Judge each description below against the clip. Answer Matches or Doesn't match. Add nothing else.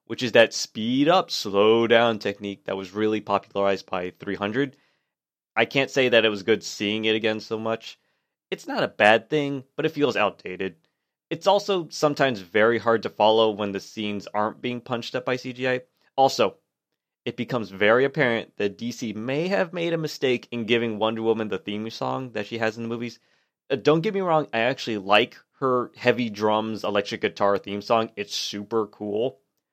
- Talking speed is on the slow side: Doesn't match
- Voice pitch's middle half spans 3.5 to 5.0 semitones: Matches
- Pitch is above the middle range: Doesn't match